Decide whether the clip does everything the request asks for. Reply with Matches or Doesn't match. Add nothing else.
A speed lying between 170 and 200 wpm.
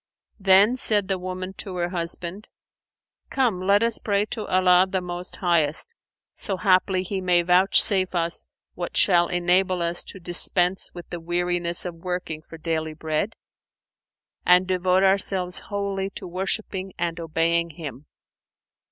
Doesn't match